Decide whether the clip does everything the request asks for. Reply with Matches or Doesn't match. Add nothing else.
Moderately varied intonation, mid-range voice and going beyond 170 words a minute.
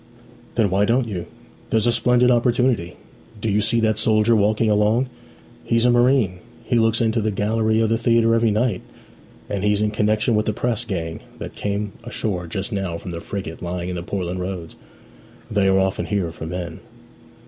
Doesn't match